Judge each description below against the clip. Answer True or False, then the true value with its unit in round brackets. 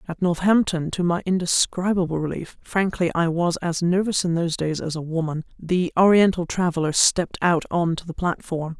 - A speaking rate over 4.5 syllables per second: False (3.7 syllables/s)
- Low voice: False (170 Hz)